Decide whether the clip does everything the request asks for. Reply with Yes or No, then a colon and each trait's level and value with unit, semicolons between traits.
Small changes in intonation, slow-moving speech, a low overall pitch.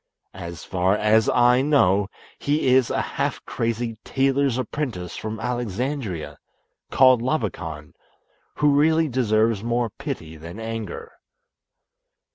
No: average, 4.5 semitones; slow, 110 wpm; low, 115 Hz